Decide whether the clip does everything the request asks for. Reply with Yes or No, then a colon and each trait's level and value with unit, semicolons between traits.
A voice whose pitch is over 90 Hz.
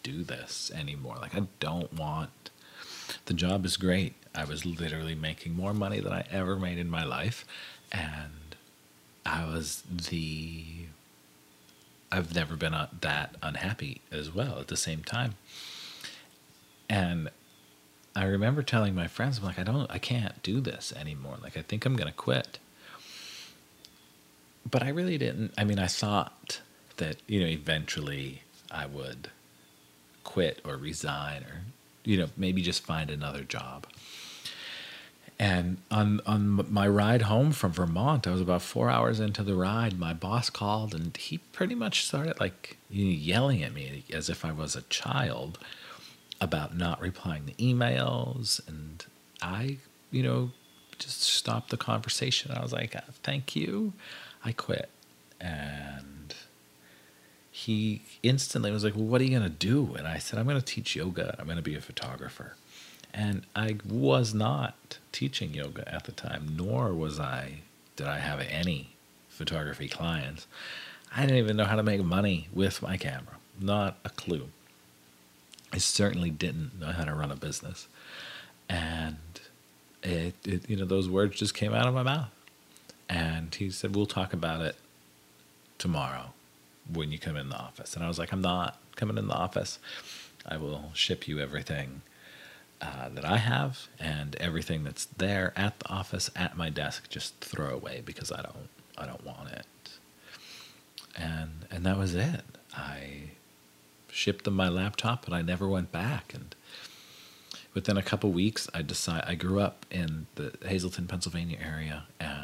No: very low, 85 Hz